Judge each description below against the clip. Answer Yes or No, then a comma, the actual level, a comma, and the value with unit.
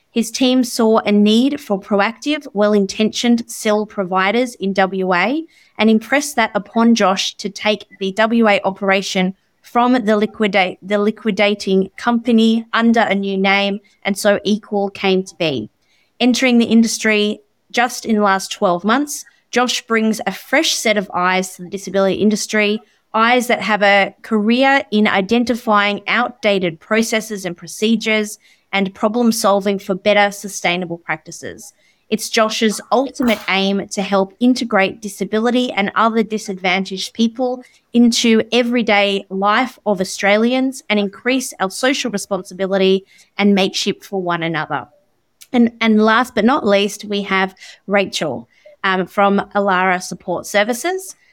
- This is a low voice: No, high, 210 Hz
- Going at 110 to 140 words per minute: Yes, slow, 135 wpm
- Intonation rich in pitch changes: No, average, 2.9 semitones